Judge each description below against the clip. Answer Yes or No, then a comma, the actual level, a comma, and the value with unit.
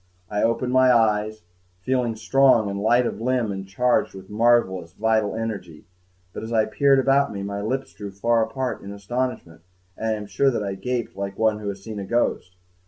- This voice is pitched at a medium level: No, low, 110 Hz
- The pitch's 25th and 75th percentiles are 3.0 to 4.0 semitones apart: Yes, average, 3.5 semitones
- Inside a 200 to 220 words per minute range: Yes, fast, 205 wpm